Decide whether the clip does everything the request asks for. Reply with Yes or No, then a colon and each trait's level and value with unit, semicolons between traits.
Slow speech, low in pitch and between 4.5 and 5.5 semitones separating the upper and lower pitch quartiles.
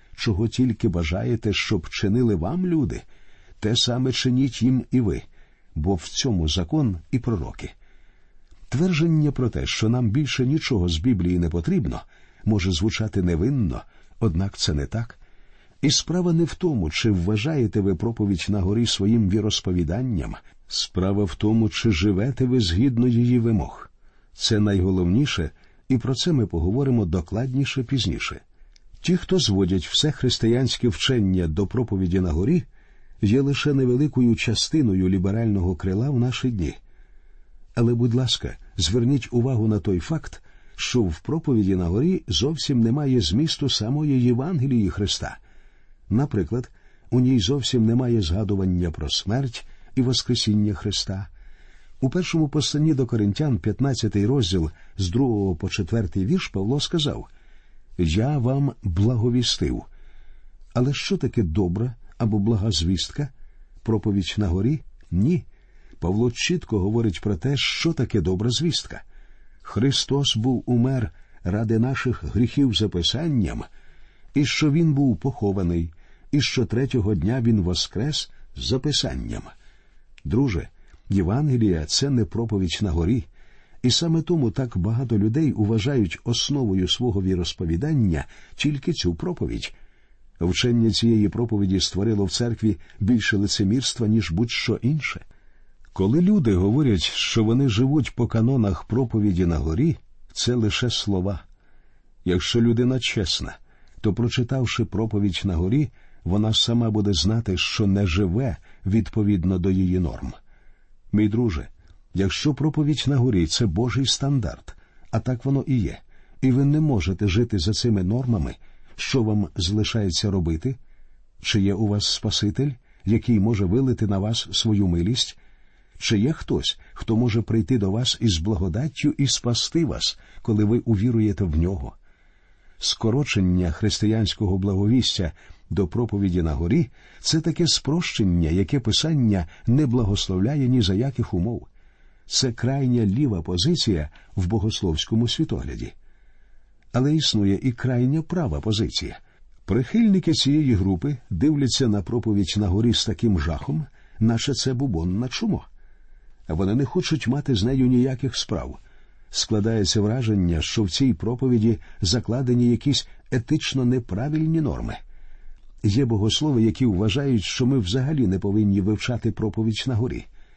No: average, 130 wpm; low, 110 Hz; average, 4.9 semitones